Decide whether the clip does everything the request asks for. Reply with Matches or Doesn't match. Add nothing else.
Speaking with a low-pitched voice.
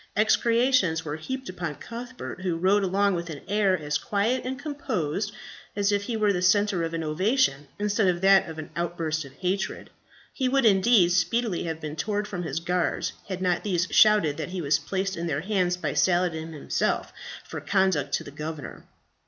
Doesn't match